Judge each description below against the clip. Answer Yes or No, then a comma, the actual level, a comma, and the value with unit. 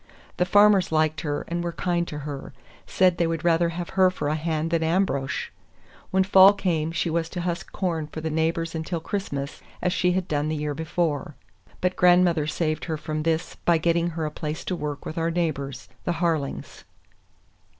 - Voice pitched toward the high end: No, medium, 165 Hz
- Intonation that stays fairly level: Yes, narrow, 2.2 semitones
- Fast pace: No, average, 195 wpm